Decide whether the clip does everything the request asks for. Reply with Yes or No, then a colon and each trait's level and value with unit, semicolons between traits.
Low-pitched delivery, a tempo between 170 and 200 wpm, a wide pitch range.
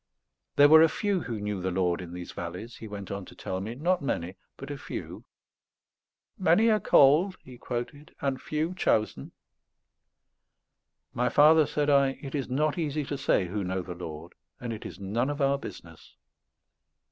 Yes: low, 130 Hz; average, 180 wpm; wide, 7.7 semitones